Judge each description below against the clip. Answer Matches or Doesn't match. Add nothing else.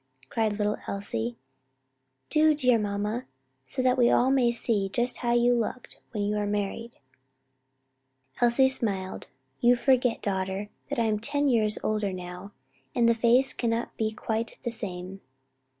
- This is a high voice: Matches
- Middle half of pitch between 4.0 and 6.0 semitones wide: Doesn't match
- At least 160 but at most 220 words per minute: Doesn't match